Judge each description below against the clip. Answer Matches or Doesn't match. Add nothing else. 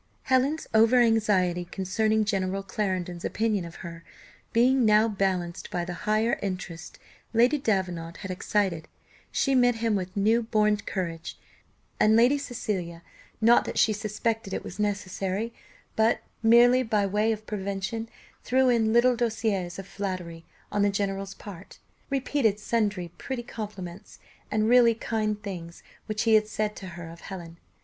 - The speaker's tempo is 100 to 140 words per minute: Doesn't match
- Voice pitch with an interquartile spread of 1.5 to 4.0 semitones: Matches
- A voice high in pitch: Matches